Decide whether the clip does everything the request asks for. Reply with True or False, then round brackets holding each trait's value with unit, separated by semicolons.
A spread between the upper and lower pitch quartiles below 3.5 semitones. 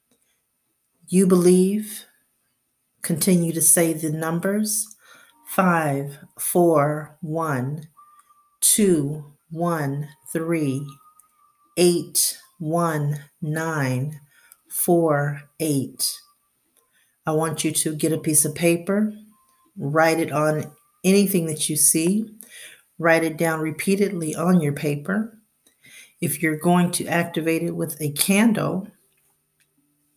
False (4.0 semitones)